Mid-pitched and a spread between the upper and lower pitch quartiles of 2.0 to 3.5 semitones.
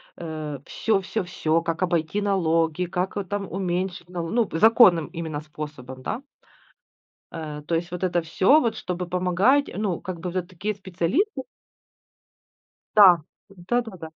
Yes: medium, 180 Hz; average, 3.2 semitones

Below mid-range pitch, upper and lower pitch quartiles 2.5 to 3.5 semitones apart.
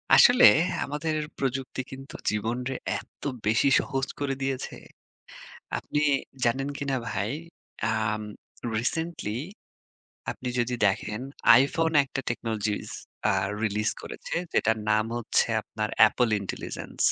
No: low, 125 Hz; average, 4.0 semitones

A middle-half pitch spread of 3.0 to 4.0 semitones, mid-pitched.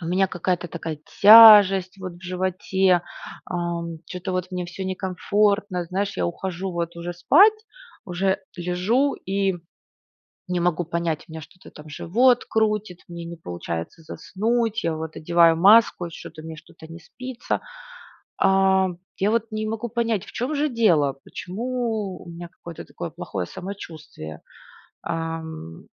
Yes: average, 3.5 semitones; medium, 180 Hz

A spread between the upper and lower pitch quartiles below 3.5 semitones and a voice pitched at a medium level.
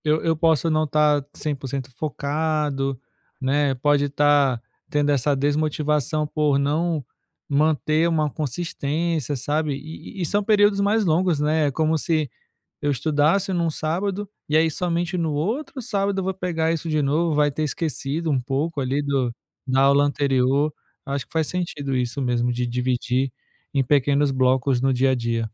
Yes: average, 2.8 semitones; medium, 150 Hz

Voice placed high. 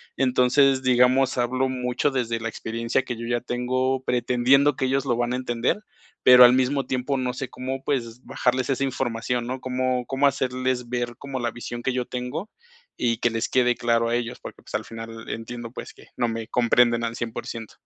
No: low, 125 Hz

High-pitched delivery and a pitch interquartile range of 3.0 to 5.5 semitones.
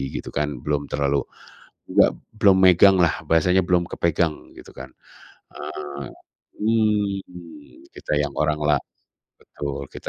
No: very low, 75 Hz; average, 4.0 semitones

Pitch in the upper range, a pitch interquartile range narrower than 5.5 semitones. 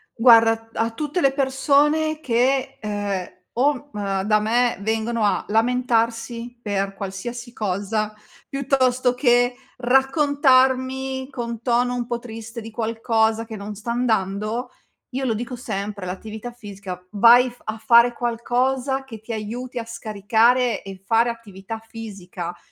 Yes: high, 235 Hz; average, 2.7 semitones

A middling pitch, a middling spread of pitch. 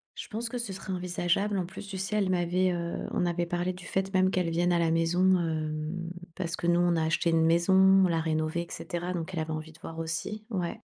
No: medium, 175 Hz; narrow, 2.2 semitones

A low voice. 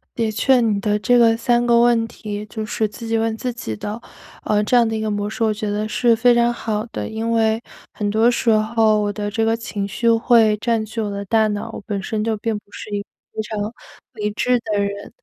No: high, 220 Hz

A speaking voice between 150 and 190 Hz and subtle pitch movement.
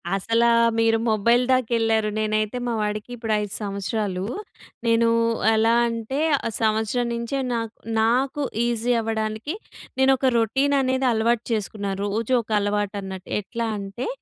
No: high, 225 Hz; narrow, 2.0 semitones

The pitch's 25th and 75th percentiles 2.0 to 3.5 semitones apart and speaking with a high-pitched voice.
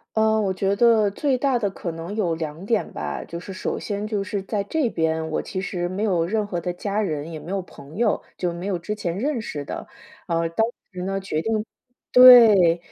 No: average, 4.2 semitones; high, 195 Hz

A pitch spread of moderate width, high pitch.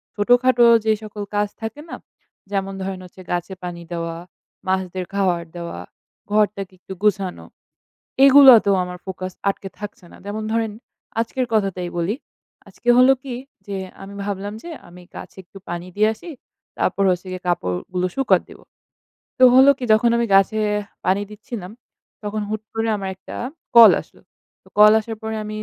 Yes: average, 3.2 semitones; high, 200 Hz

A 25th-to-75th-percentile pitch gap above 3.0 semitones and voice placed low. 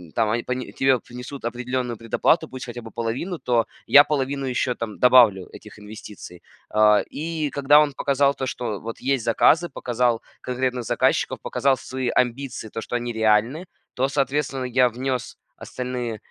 No: average, 2.7 semitones; low, 125 Hz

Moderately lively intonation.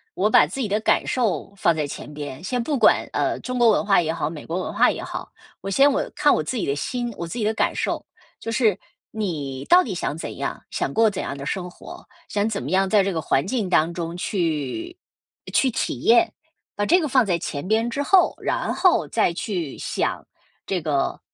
No: wide, 6.3 semitones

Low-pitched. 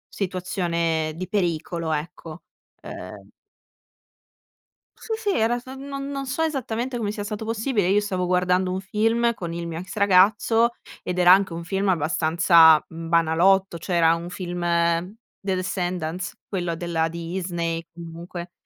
No: medium, 180 Hz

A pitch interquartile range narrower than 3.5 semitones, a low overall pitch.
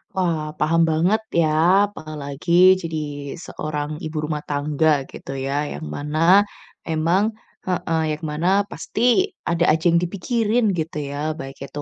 No: average, 2.9 semitones; medium, 155 Hz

